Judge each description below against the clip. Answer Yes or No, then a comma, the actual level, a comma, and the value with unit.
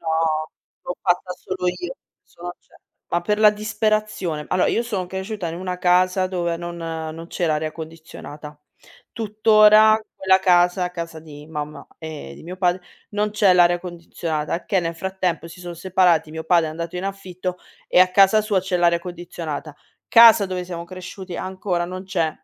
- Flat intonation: Yes, narrow, 2.2 semitones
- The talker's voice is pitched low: No, medium, 180 Hz